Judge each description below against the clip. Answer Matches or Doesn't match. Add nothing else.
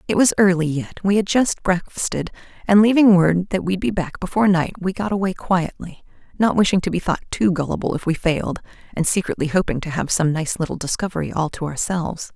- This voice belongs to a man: Doesn't match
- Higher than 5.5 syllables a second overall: Matches